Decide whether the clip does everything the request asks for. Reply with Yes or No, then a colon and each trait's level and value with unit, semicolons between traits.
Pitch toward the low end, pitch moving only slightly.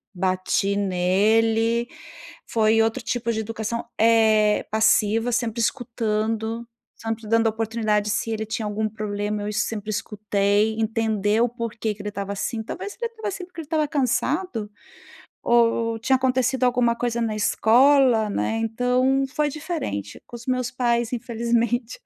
No: high, 225 Hz; narrow, 2.2 semitones